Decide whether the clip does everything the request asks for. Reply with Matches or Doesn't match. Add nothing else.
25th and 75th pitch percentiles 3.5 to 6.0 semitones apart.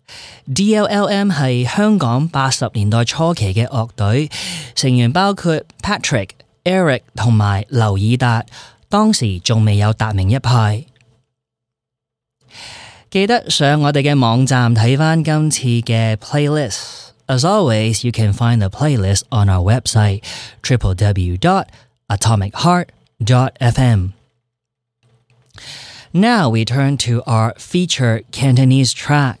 Matches